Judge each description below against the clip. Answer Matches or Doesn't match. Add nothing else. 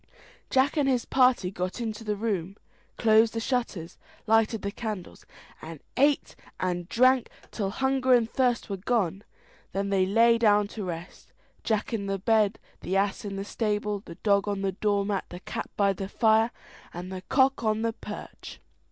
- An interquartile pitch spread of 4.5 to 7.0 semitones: Doesn't match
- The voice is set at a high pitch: Matches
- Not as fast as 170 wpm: Doesn't match